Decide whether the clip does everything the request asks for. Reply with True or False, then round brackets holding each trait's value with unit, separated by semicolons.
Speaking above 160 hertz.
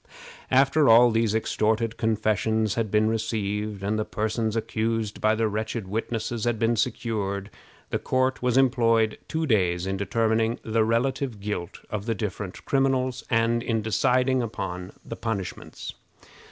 False (110 Hz)